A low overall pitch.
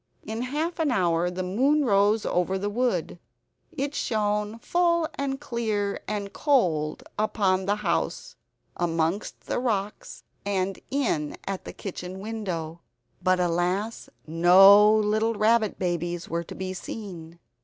No: high, 200 Hz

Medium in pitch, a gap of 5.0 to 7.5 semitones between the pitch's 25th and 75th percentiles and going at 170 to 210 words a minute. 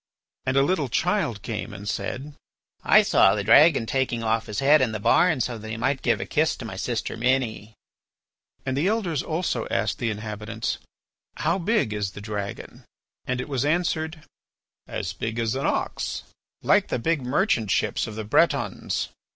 No: low, 125 Hz; wide, 5.5 semitones; average, 180 wpm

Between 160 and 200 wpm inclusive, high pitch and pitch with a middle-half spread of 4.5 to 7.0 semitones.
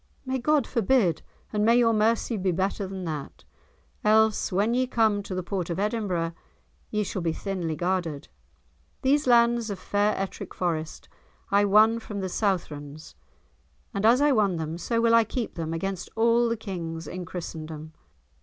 Yes: average, 170 wpm; high, 200 Hz; average, 4.8 semitones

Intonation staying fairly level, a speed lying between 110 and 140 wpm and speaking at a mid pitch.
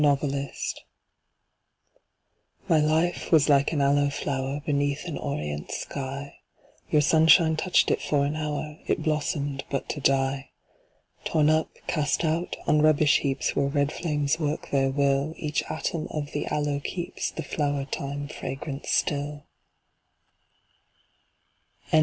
Yes: narrow, 1.7 semitones; slow, 135 wpm; medium, 145 Hz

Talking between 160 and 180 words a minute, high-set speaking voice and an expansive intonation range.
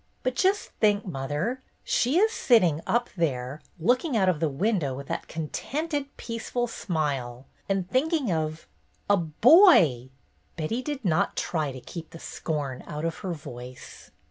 No: average, 165 wpm; medium, 170 Hz; wide, 8.7 semitones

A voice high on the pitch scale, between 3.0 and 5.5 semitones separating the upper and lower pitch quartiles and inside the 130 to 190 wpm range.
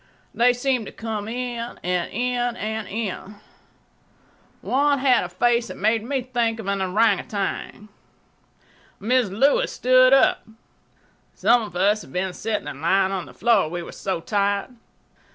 Yes: high, 220 Hz; average, 3.8 semitones; average, 150 wpm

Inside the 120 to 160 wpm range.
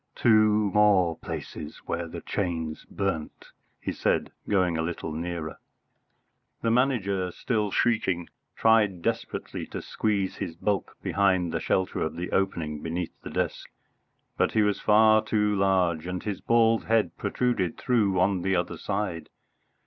Yes: average, 145 wpm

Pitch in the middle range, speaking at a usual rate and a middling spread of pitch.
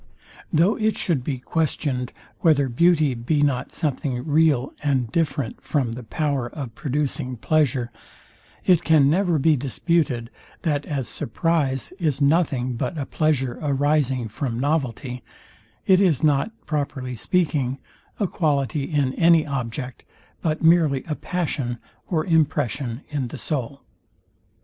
No: medium, 145 Hz; slow, 130 wpm; average, 3.8 semitones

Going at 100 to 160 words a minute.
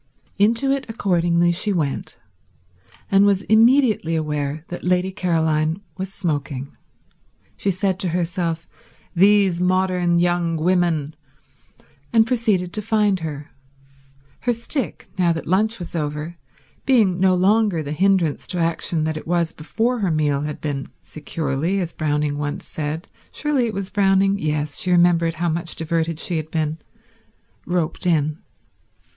Yes: average, 140 wpm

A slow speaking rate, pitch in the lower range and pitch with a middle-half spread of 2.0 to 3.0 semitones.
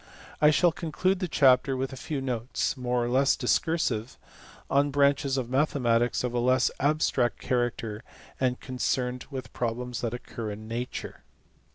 No: average, 155 wpm; low, 125 Hz; narrow, 2.4 semitones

